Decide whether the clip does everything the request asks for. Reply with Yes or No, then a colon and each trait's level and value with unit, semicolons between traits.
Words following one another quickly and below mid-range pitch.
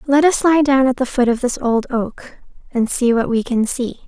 No: fast, 250 wpm; very high, 255 Hz